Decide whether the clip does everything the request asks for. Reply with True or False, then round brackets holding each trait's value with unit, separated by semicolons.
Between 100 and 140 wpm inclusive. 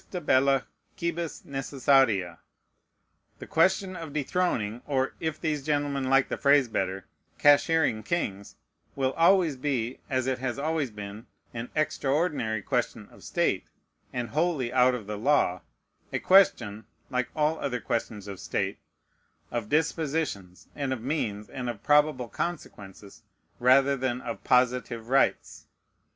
True (135 wpm)